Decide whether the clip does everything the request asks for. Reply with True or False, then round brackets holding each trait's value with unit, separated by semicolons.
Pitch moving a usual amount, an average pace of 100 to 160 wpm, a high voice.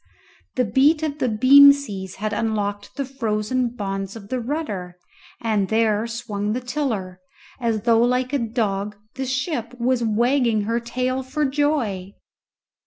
True (3.8 semitones; 150 wpm; 235 Hz)